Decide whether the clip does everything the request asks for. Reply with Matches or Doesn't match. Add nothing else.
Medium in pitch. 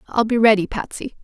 Doesn't match